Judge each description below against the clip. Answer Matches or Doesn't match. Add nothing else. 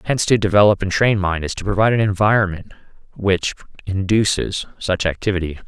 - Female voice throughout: Doesn't match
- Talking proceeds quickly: Doesn't match